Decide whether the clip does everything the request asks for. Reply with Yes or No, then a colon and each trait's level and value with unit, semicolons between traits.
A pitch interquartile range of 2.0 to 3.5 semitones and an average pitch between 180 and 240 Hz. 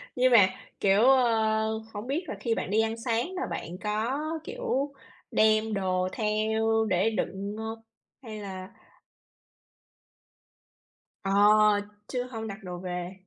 Yes: average, 2.8 semitones; high, 220 Hz